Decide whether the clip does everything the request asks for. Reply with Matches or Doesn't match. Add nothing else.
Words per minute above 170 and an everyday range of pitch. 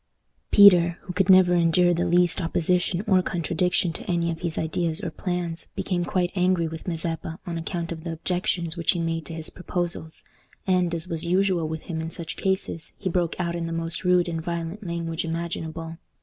Doesn't match